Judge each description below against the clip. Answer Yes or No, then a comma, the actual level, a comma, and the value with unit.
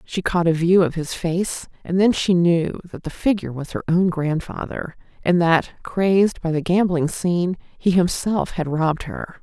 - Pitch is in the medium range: Yes, medium, 175 Hz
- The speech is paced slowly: No, average, 190 wpm